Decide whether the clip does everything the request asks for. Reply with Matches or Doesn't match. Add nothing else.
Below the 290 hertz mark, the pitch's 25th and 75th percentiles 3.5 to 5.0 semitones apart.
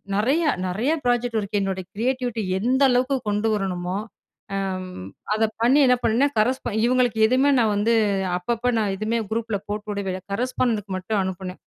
Matches